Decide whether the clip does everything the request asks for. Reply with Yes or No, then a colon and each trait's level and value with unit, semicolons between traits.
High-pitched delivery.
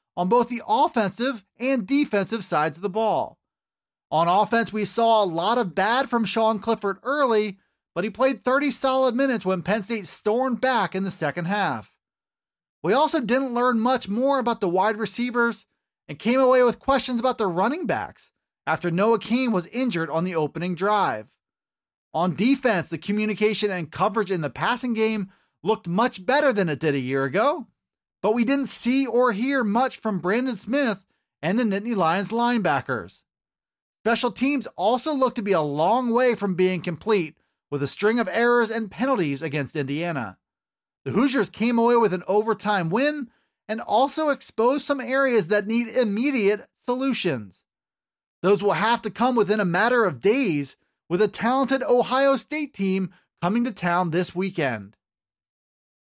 Yes: high, 220 Hz